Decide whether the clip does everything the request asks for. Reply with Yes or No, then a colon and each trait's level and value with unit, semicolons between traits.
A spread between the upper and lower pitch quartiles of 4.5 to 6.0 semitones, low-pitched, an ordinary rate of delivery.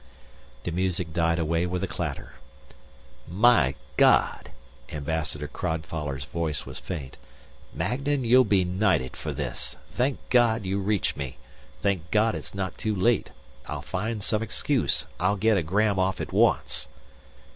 Yes: average, 5.0 semitones; very low, 90 Hz; average, 145 wpm